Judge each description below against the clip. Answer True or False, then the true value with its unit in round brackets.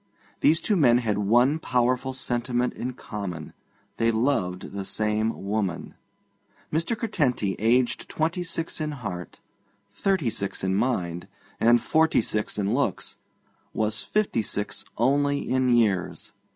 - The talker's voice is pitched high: False (120 Hz)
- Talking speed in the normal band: False (130 wpm)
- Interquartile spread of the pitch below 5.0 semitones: False (5.4 semitones)